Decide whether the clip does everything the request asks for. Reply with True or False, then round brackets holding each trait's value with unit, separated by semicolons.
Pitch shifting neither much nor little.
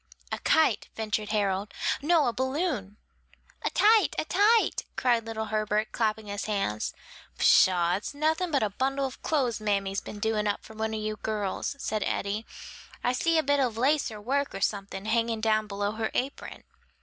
True (4.6 semitones)